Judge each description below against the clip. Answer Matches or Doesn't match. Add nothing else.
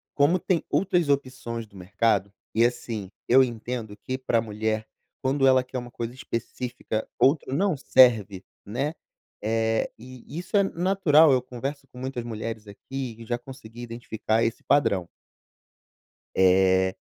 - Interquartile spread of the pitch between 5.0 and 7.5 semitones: Doesn't match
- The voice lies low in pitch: Matches